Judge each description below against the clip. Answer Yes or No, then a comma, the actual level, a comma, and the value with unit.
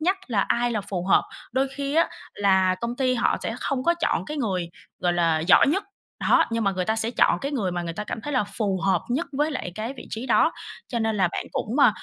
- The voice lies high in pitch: Yes, high, 225 Hz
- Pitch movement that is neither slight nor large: No, wide, 6.0 semitones